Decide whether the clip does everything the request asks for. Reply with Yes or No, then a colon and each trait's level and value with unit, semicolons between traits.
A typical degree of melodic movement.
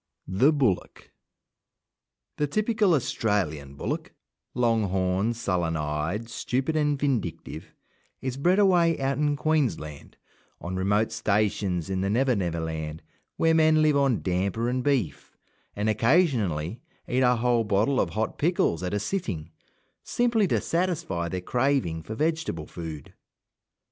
No: wide, 8.1 semitones